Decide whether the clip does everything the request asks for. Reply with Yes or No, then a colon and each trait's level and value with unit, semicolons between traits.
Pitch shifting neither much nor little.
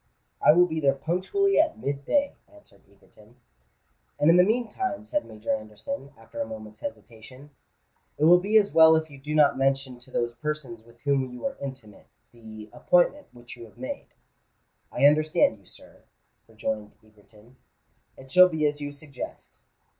No: wide, 7.1 semitones